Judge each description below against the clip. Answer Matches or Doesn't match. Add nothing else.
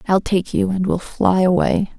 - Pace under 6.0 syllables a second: Matches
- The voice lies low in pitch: Doesn't match